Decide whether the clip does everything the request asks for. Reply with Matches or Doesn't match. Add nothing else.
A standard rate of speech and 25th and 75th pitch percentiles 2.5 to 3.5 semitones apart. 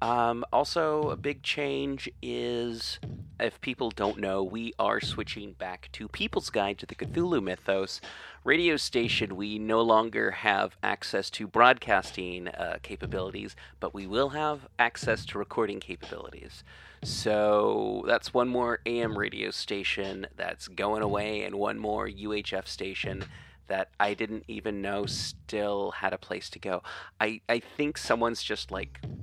Matches